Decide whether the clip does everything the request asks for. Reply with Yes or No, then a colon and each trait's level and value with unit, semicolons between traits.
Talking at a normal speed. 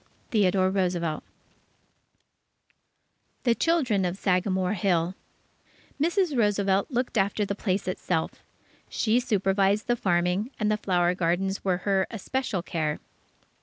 No: slow, 115 wpm